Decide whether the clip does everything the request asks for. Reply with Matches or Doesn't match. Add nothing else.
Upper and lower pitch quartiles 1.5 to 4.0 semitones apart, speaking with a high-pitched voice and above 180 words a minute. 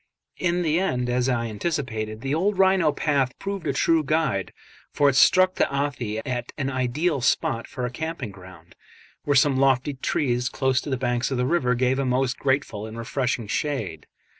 Doesn't match